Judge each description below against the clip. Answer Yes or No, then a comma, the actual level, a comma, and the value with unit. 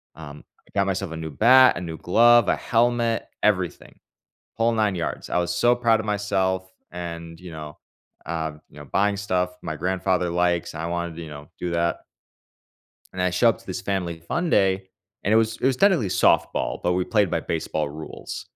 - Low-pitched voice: Yes, very low, 90 Hz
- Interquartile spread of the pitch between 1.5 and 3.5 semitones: No, average, 4.0 semitones